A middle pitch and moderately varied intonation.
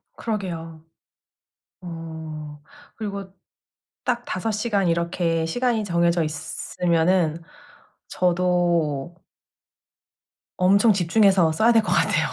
Yes: medium, 175 Hz; average, 3.5 semitones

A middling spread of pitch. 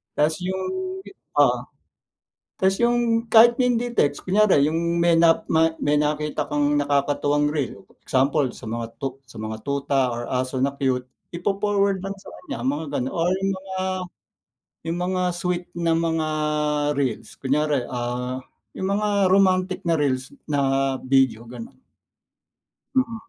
No: wide, 5.8 semitones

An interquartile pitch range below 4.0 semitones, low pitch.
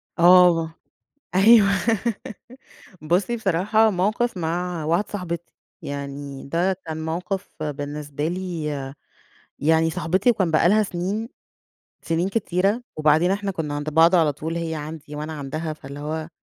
No: average, 3.5 semitones; medium, 165 Hz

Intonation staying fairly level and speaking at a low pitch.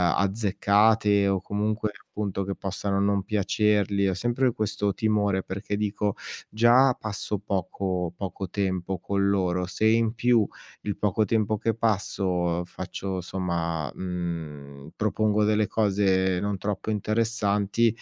Yes: narrow, 2.3 semitones; low, 100 Hz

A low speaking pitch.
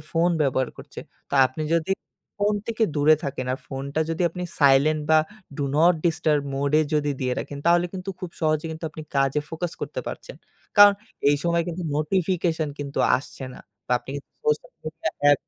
No: medium, 155 Hz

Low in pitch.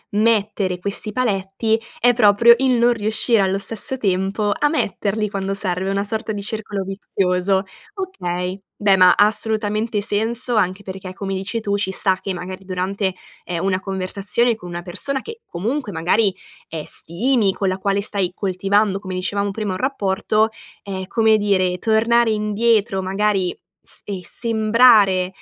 No: high, 200 Hz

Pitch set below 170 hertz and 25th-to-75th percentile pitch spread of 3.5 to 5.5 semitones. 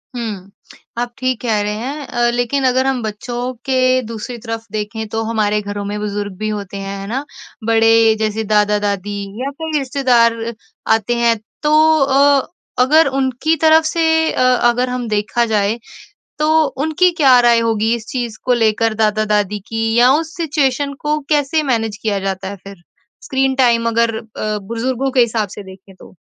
No: high, 230 Hz; average, 3.9 semitones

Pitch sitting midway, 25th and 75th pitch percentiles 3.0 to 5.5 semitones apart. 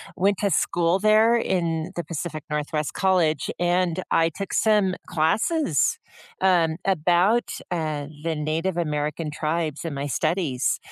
Yes: medium, 170 Hz; average, 3.4 semitones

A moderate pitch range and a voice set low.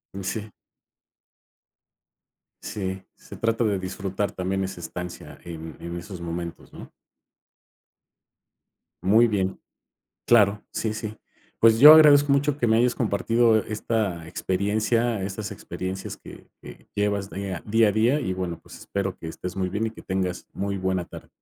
Yes: average, 3.2 semitones; low, 100 Hz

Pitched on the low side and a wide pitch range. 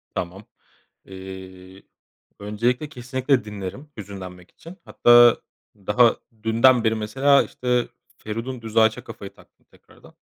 No: low, 110 Hz; average, 4.0 semitones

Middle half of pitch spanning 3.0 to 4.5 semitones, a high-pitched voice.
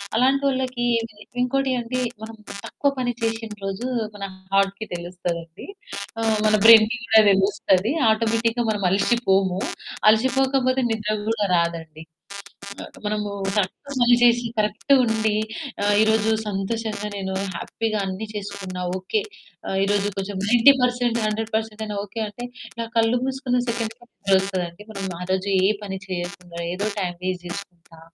Yes: average, 3.3 semitones; high, 215 Hz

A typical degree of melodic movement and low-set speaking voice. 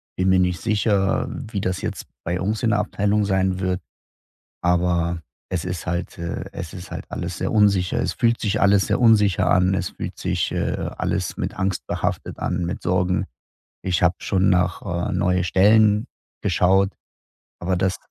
No: narrow, 2.1 semitones; very low, 95 Hz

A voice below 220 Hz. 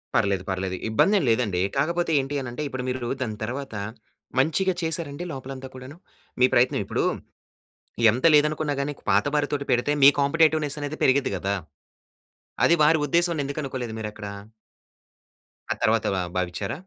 Yes: low, 135 Hz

